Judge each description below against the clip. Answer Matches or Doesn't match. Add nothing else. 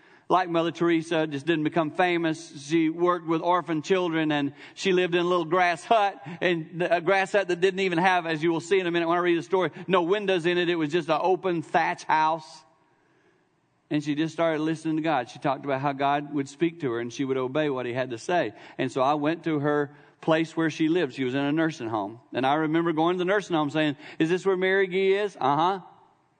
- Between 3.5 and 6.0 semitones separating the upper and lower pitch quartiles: Doesn't match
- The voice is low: Doesn't match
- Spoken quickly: Matches